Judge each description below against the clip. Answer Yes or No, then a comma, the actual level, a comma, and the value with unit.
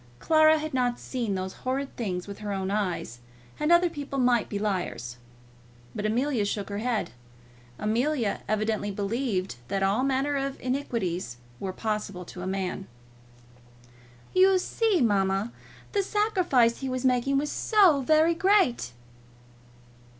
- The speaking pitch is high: Yes, high, 240 Hz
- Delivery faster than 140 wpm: No, slow, 135 wpm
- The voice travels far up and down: Yes, wide, 6.3 semitones